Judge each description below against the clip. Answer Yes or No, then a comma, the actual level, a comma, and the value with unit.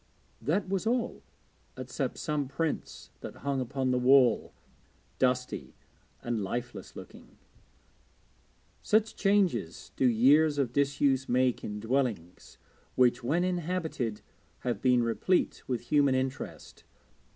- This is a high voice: No, low, 130 Hz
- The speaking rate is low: Yes, slow, 115 wpm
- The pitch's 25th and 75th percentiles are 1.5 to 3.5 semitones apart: No, average, 4.0 semitones